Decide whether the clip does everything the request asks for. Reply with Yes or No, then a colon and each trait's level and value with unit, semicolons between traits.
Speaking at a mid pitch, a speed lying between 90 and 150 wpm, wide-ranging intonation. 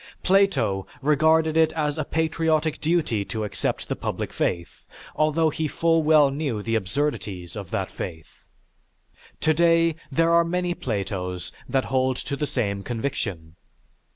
Yes: medium, 145 Hz; average, 140 wpm; wide, 7.3 semitones